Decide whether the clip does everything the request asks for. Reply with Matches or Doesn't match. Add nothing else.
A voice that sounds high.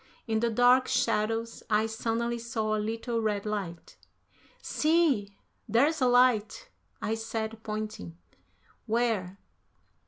Matches